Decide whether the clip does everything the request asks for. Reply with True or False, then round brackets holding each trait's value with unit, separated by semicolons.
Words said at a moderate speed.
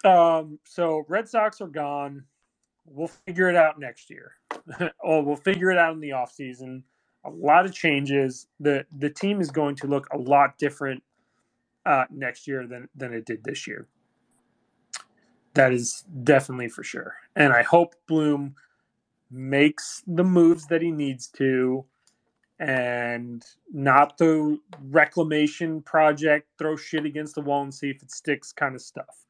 True (160 wpm)